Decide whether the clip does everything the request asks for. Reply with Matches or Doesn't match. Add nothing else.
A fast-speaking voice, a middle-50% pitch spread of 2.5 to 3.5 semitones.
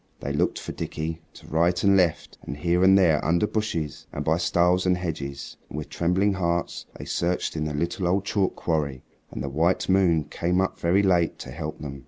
Matches